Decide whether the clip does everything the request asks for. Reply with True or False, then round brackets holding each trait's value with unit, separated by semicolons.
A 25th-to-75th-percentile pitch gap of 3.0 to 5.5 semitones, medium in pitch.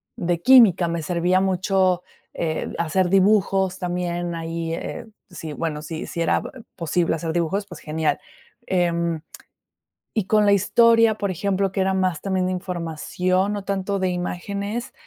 False (2.5 semitones; 180 Hz)